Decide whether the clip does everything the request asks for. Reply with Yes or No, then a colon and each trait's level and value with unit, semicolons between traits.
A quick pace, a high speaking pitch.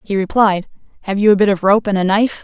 Yes: fast, 270 wpm; high, 200 Hz